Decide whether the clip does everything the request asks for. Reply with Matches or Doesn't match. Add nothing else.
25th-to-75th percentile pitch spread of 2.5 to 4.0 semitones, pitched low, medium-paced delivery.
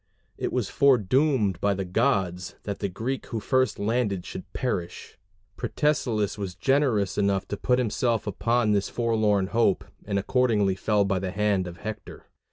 Matches